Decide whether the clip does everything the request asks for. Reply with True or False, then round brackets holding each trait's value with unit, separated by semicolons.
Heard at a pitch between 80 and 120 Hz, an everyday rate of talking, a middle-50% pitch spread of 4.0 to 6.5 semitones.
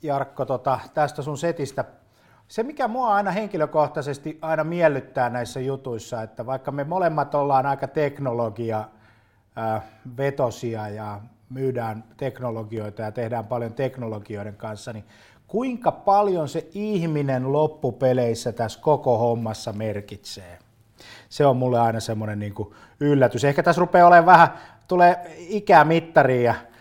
False (130 Hz; 120 wpm; 5.2 semitones)